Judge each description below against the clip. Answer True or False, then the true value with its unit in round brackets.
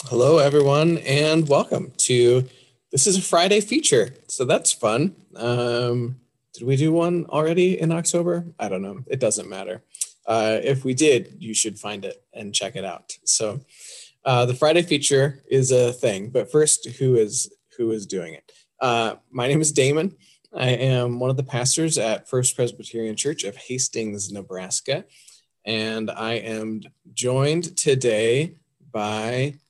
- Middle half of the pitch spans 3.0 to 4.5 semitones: False (4.9 semitones)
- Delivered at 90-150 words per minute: False (160 wpm)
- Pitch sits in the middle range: False (130 Hz)